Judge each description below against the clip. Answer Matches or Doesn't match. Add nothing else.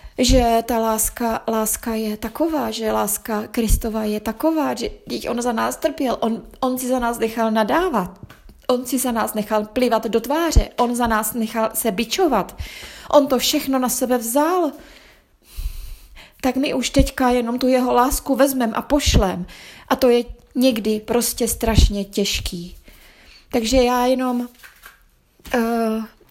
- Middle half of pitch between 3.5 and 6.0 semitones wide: Doesn't match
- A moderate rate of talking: Matches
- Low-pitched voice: Doesn't match